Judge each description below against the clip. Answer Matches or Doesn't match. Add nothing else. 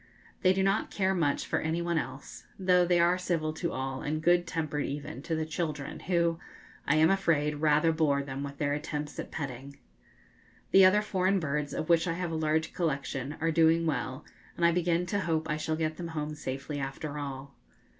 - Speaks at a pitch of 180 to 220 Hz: Doesn't match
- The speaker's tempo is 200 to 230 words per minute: Matches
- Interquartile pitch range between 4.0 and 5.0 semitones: Doesn't match